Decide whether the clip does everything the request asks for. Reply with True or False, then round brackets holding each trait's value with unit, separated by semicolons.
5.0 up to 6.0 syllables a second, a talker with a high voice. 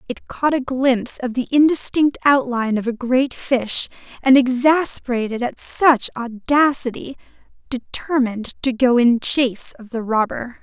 False (4.5 syllables/s; 250 Hz)